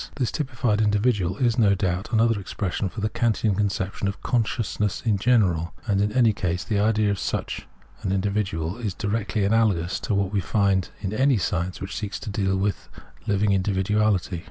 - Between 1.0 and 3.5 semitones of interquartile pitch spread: Yes, narrow, 2.4 semitones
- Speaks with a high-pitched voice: No, low, 100 Hz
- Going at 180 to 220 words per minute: Yes, average, 190 wpm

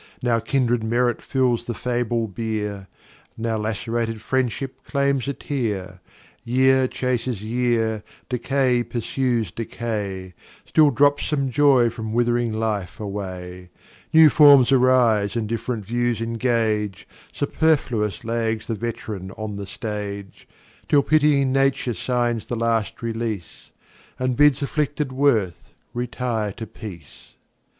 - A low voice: Yes, low, 115 Hz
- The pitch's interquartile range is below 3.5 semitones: Yes, average, 3.0 semitones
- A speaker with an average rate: No, slow, 120 wpm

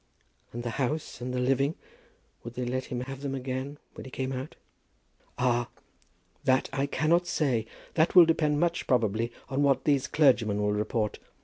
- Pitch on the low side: Yes, low, 130 Hz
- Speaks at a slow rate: No, average, 175 wpm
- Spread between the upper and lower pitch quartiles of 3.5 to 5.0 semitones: No, average, 2.9 semitones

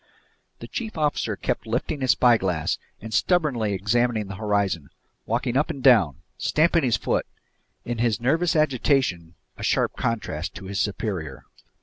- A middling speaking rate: Yes, average, 145 wpm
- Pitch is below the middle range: Yes, low, 115 Hz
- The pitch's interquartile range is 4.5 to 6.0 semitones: Yes, wide, 5.5 semitones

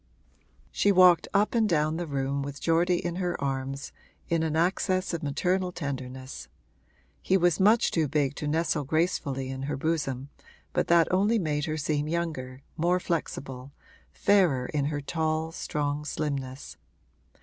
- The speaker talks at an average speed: Yes, average, 150 wpm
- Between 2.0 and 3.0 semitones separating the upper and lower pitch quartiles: No, average, 3.9 semitones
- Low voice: No, medium, 155 Hz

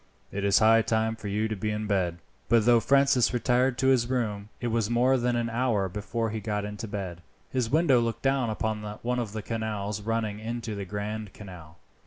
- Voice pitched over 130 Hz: No, low, 110 Hz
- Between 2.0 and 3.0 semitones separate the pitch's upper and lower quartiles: Yes, narrow, 2.5 semitones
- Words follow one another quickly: Yes, fast, 210 wpm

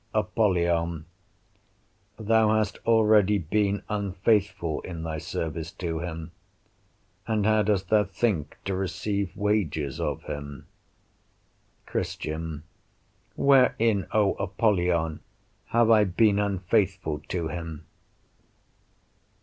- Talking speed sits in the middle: No, slow, 95 wpm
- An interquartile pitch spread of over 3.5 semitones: Yes, average, 4.4 semitones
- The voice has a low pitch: Yes, very low, 95 Hz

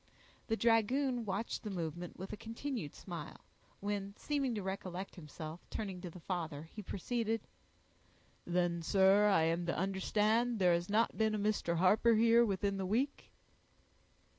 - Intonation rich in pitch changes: No, average, 4.1 semitones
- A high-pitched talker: Yes, high, 200 Hz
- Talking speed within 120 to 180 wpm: Yes, average, 155 wpm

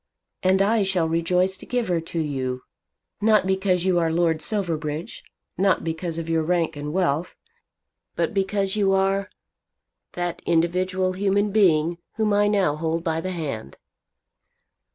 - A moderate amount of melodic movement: Yes, average, 3.0 semitones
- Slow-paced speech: No, average, 150 wpm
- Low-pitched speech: No, medium, 180 Hz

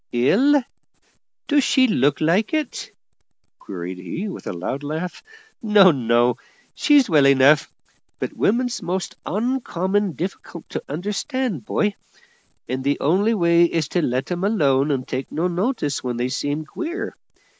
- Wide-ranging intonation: Yes, wide, 7.5 semitones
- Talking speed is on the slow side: No, average, 145 wpm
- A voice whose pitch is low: No, medium, 170 Hz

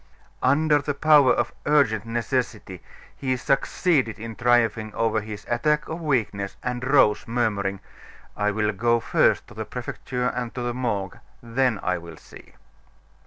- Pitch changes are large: No, average, 3.5 semitones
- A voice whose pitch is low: Yes, low, 120 Hz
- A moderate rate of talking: Yes, average, 150 wpm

